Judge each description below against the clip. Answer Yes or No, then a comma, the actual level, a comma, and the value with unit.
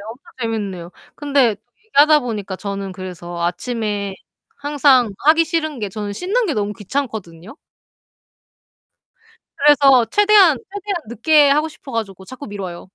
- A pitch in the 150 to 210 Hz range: No, high, 235 Hz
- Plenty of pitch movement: Yes, wide, 6.7 semitones